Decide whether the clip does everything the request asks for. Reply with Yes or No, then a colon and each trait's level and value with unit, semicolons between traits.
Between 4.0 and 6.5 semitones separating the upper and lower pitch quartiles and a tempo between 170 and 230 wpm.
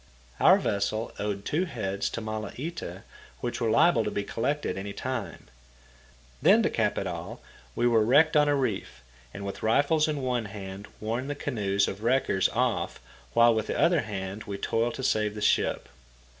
Yes: average, 4.6 semitones; average, 180 wpm